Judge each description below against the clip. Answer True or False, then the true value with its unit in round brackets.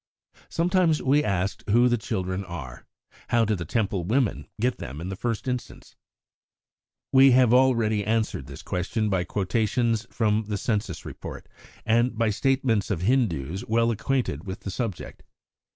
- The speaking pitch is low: True (110 Hz)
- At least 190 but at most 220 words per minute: False (155 wpm)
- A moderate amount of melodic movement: True (4.2 semitones)